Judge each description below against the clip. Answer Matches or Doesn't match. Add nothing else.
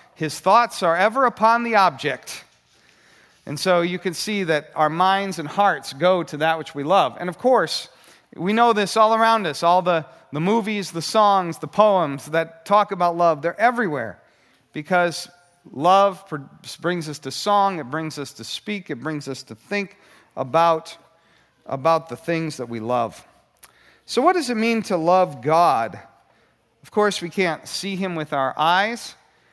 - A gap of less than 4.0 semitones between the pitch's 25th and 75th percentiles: Doesn't match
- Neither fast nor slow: Matches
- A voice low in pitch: Doesn't match